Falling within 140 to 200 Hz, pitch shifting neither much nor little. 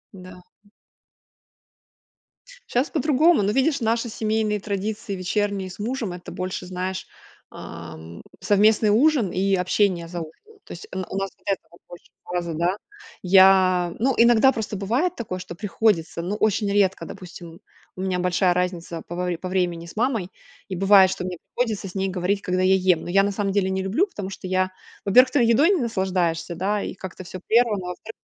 Yes: high, 190 Hz; average, 3.1 semitones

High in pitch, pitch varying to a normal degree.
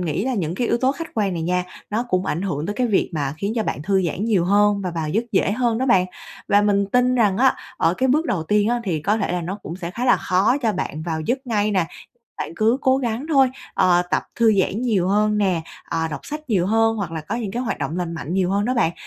Yes: high, 205 Hz; average, 4.7 semitones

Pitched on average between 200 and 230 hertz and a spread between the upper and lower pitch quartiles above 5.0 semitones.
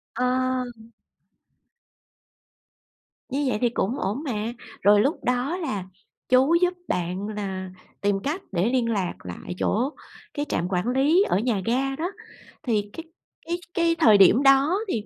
No: high, 245 Hz; wide, 5.6 semitones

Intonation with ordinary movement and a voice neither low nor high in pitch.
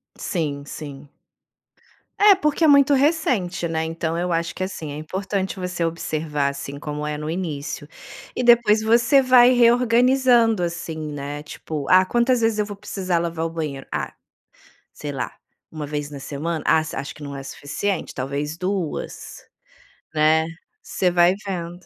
No: wide, 6.3 semitones; medium, 170 Hz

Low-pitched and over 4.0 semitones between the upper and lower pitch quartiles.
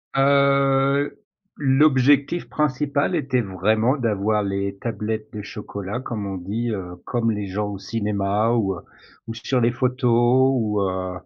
Yes: low, 115 Hz; average, 4.7 semitones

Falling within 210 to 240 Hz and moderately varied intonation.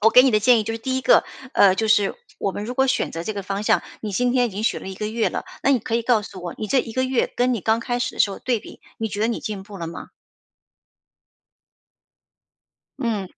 Yes: high, 220 Hz; average, 3.3 semitones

